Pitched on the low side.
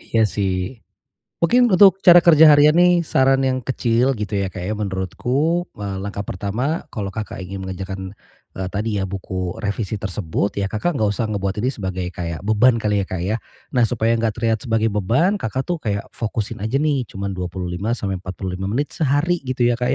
Yes: low, 110 Hz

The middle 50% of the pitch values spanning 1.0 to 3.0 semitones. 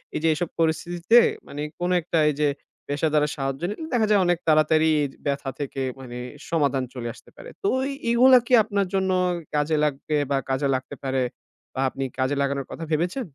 No: average, 4.3 semitones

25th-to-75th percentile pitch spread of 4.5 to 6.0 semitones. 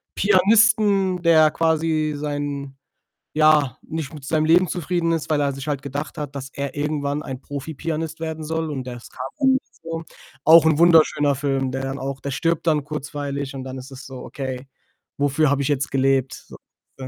No: average, 2.9 semitones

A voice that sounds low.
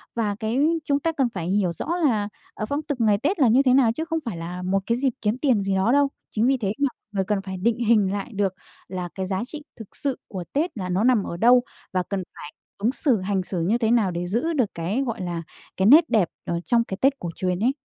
No: high, 220 Hz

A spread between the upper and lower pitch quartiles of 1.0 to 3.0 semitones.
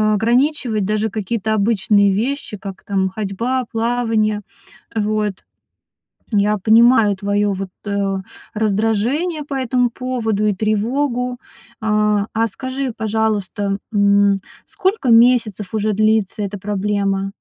Yes: average, 2.7 semitones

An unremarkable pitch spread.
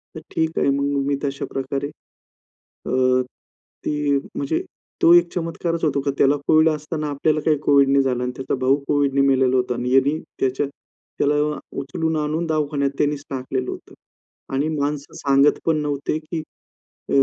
No: narrow, 2.1 semitones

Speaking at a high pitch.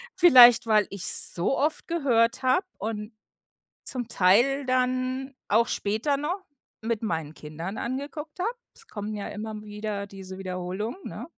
Yes: high, 225 Hz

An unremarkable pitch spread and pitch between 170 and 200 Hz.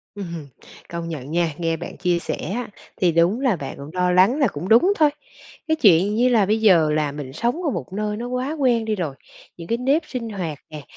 No: wide, 6.3 semitones; high, 190 Hz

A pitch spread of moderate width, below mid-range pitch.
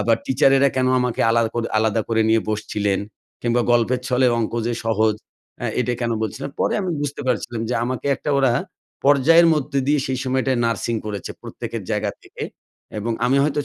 Yes: average, 3.0 semitones; low, 125 Hz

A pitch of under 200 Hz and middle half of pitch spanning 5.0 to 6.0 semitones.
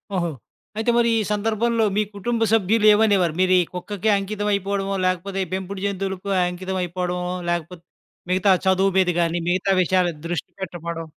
No: high, 190 Hz; narrow, 2.4 semitones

